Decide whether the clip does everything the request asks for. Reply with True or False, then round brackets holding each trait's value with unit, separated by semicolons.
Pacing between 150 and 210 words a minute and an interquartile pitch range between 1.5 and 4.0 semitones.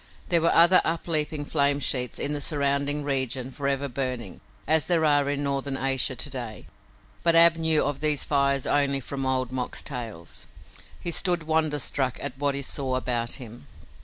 True (170 wpm; 2.5 semitones)